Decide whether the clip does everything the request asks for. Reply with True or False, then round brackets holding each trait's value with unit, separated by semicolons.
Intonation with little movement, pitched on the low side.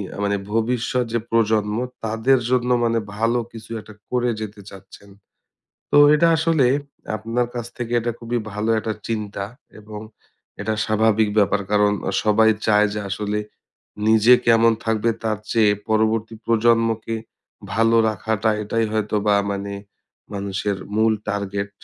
True (1.7 semitones; 110 Hz)